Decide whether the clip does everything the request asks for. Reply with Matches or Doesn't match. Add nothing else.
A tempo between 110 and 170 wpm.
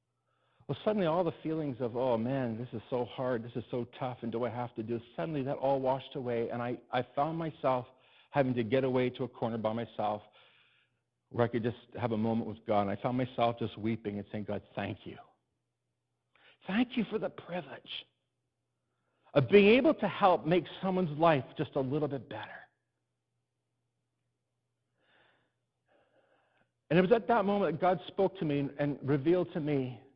Doesn't match